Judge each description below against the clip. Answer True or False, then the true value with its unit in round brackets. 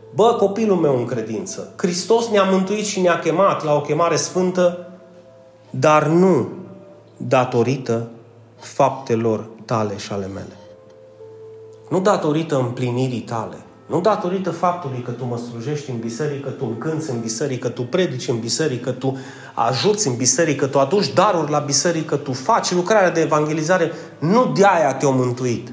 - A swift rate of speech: False (160 wpm)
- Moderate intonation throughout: False (6.3 semitones)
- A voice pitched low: False (145 Hz)